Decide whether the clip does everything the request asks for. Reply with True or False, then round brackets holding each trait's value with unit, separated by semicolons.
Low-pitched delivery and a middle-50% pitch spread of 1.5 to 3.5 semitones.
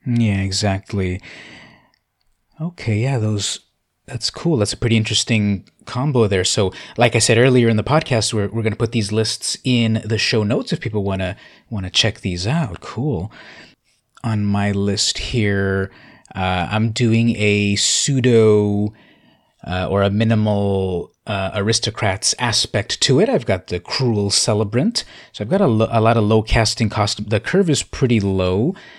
True (110 Hz; 2.5 semitones)